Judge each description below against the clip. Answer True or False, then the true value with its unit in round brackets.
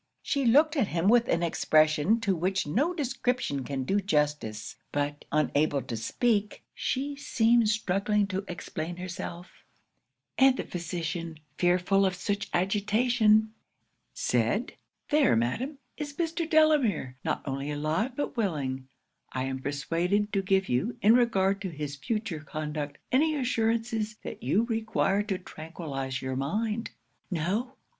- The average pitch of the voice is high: True (195 Hz)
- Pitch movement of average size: False (7.0 semitones)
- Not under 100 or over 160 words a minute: True (135 wpm)